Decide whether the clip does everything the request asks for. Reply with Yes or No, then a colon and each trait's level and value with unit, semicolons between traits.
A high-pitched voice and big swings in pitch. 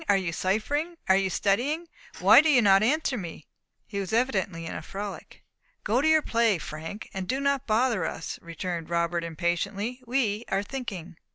Yes: high, 200 Hz; wide, 6.0 semitones